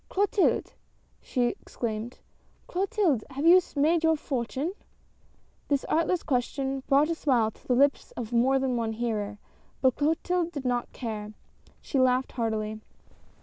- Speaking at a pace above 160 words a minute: No, average, 155 wpm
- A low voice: No, very high, 265 Hz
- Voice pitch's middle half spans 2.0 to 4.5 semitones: No, average, 5.0 semitones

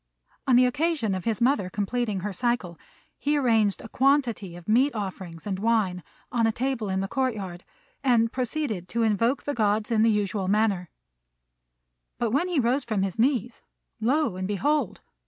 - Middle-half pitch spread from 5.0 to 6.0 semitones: No, average, 4.5 semitones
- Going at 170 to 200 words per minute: Yes, average, 175 wpm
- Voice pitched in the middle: No, high, 225 Hz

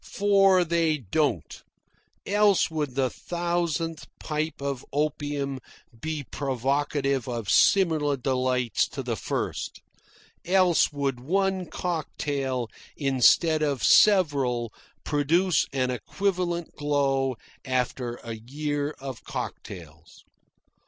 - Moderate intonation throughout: Yes, average, 4.5 semitones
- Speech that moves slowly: Yes, slow, 100 wpm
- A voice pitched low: No, medium, 145 Hz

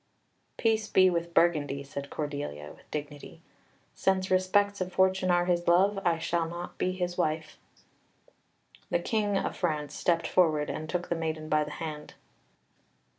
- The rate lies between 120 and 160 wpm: Yes, average, 155 wpm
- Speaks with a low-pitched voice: No, medium, 170 Hz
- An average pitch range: Yes, average, 3.3 semitones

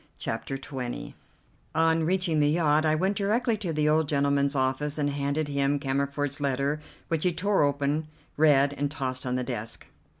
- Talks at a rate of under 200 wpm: Yes, average, 170 wpm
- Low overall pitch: No, medium, 145 Hz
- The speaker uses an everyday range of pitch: No, narrow, 2.3 semitones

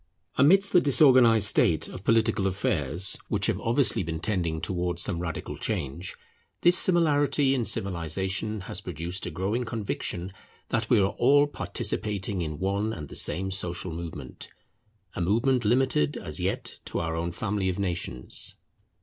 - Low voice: Yes, very low, 95 Hz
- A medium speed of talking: Yes, average, 150 wpm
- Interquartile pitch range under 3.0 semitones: No, average, 5.3 semitones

